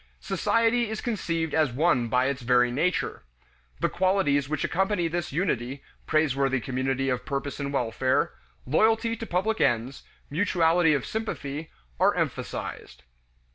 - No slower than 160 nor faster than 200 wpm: No, slow, 135 wpm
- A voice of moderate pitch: Yes, medium, 150 Hz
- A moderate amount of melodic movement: No, wide, 5.7 semitones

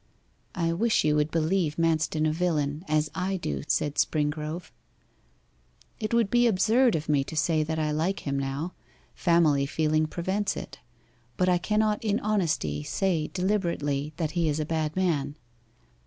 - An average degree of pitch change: Yes, average, 3.7 semitones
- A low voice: No, medium, 160 Hz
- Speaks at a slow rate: No, average, 160 wpm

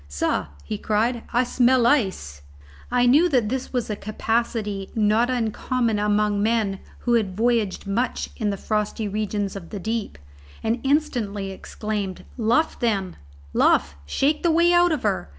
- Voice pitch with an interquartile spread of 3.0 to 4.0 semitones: Yes, average, 3.3 semitones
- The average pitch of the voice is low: No, high, 220 Hz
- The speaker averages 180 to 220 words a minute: No, average, 155 wpm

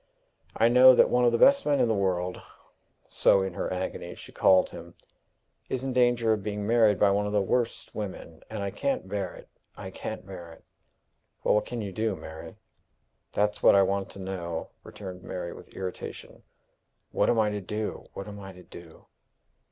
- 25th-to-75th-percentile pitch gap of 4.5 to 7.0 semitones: No, average, 3.2 semitones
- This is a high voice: No, low, 100 Hz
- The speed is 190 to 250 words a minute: Yes, average, 200 wpm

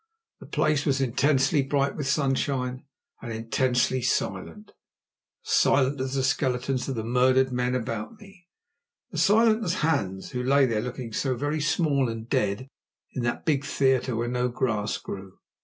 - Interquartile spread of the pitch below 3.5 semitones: Yes, average, 2.8 semitones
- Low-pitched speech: Yes, low, 130 Hz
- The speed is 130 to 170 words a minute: Yes, average, 160 wpm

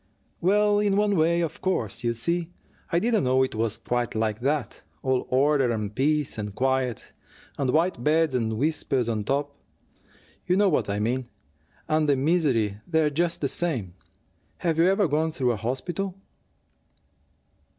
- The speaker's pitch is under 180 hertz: Yes, medium, 140 Hz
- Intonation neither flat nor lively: No, wide, 5.9 semitones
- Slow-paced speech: No, average, 160 wpm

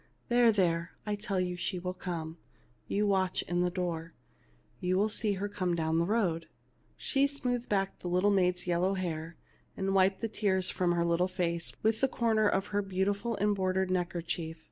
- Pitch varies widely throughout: No, average, 2.8 semitones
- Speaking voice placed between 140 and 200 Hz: Yes, medium, 185 Hz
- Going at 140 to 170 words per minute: No, average, 190 wpm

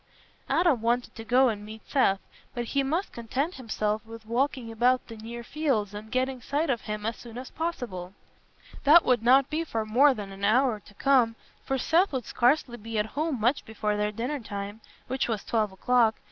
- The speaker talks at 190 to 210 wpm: Yes, average, 200 wpm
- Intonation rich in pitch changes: No, average, 3.7 semitones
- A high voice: Yes, high, 240 Hz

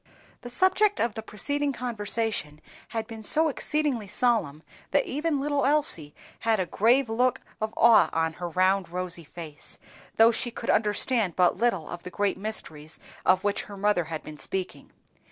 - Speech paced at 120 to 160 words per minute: No, average, 170 wpm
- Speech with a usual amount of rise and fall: No, wide, 5.9 semitones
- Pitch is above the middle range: Yes, high, 215 Hz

